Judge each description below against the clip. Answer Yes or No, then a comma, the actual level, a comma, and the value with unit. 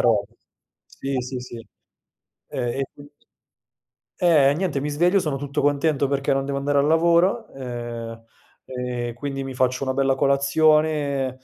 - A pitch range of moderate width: No, narrow, 2.3 semitones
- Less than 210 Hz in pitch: Yes, medium, 140 Hz